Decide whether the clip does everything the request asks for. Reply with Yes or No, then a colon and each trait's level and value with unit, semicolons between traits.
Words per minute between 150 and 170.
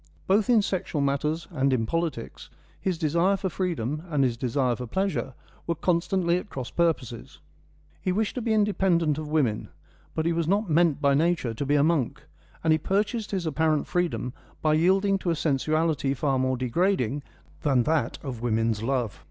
No: average, 180 wpm